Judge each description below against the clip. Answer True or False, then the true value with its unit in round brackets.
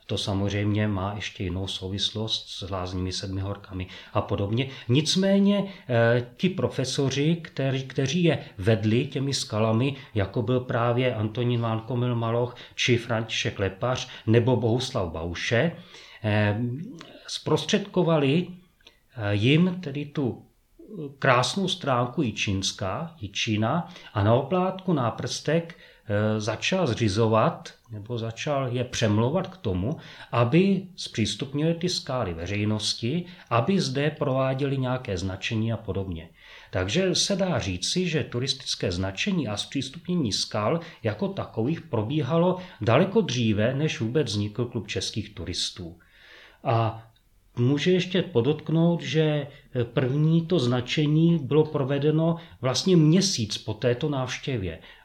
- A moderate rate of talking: False (110 wpm)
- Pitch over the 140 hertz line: False (125 Hz)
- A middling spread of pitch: False (6.3 semitones)